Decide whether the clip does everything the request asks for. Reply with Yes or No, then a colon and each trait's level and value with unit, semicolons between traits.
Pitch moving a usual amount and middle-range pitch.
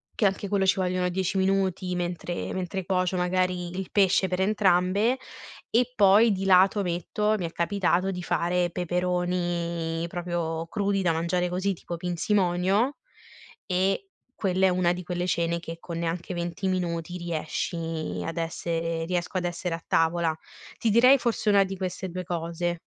No: narrow, 1.9 semitones; medium, 180 Hz